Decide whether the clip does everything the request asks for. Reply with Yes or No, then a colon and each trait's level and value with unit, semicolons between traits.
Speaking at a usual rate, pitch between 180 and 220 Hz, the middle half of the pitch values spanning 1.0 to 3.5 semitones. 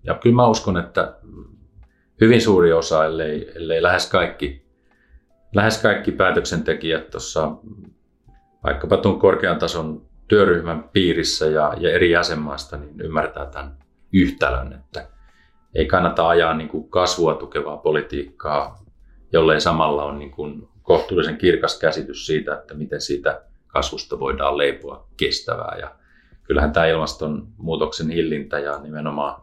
No: average, 125 wpm; very low, 75 Hz; narrow, 2.6 semitones